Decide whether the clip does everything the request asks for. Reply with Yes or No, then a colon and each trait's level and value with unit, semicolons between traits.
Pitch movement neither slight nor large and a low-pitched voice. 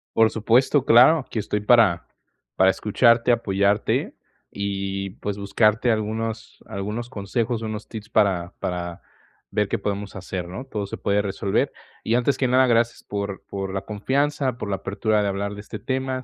Yes: average, 3.1 semitones; low, 105 Hz